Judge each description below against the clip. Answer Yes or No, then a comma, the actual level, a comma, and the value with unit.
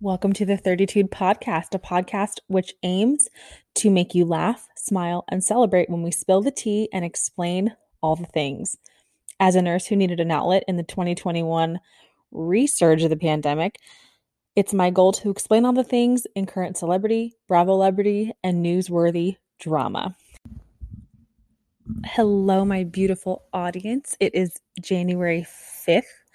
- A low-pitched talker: No, medium, 185 Hz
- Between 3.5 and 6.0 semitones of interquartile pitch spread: No, narrow, 2.6 semitones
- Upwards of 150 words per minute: No, average, 145 wpm